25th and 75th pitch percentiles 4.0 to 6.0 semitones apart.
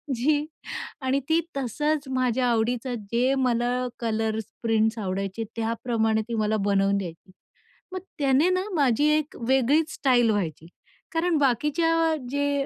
Yes: average, 4.4 semitones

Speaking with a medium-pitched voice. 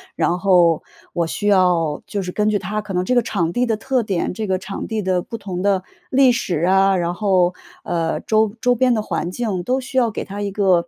No: high, 195 Hz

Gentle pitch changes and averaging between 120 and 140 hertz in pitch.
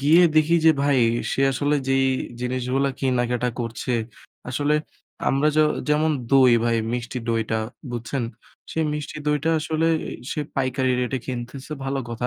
No: average, 3.2 semitones; low, 135 Hz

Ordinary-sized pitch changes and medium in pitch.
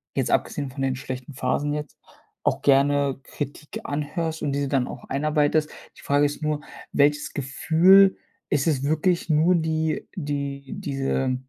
No: narrow, 2.1 semitones; medium, 145 Hz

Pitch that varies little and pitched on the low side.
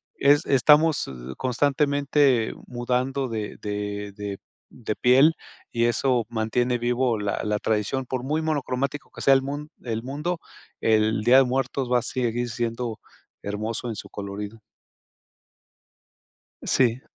No: average, 3.4 semitones; low, 125 Hz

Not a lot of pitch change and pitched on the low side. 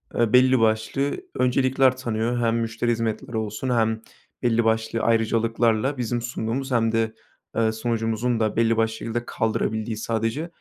Yes: narrow, 1.6 semitones; low, 115 Hz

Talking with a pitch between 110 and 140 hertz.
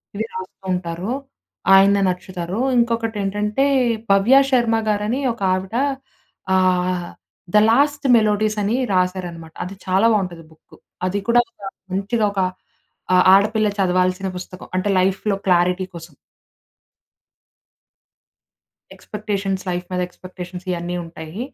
No: high, 190 Hz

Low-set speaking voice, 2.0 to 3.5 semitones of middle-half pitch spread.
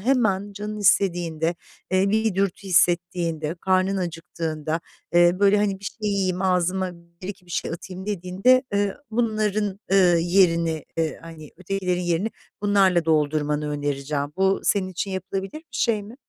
No: medium, 185 Hz; average, 2.9 semitones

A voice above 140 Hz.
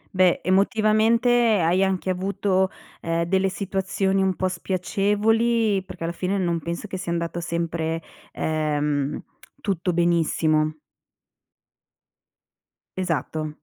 Yes: medium, 185 Hz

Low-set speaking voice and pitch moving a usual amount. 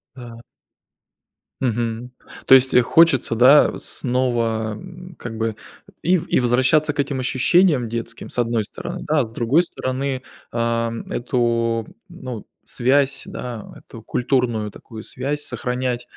Yes: low, 125 Hz; average, 3.0 semitones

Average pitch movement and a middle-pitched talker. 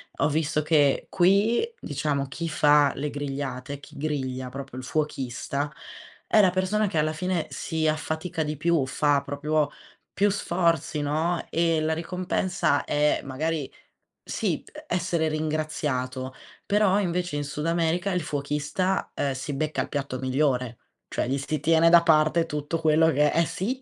Yes: average, 3.0 semitones; medium, 155 Hz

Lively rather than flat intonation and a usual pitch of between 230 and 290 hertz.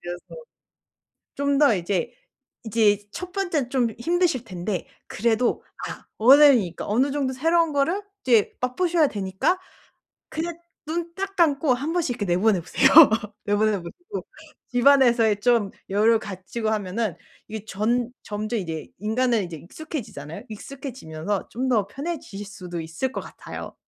Yes: wide, 5.8 semitones; high, 235 Hz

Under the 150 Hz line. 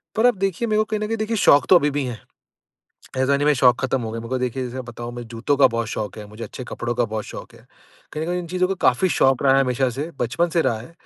Yes: low, 135 Hz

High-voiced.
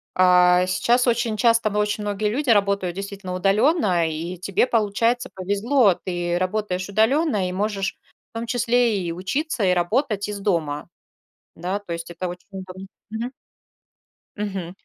Yes: high, 200 Hz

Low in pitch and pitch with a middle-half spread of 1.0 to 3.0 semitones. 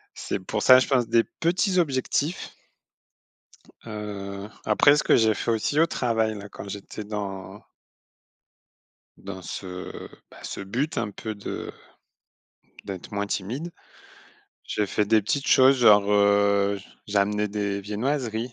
No: low, 105 Hz; average, 3.9 semitones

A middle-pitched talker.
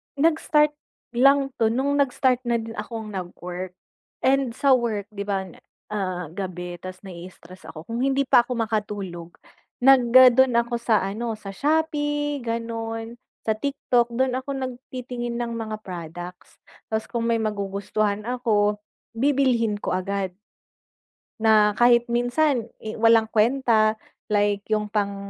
No: high, 225 Hz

